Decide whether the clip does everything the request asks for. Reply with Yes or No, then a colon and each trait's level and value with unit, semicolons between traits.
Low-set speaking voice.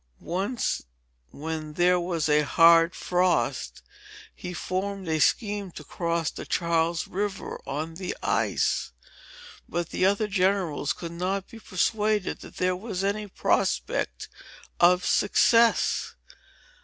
No: medium, 180 Hz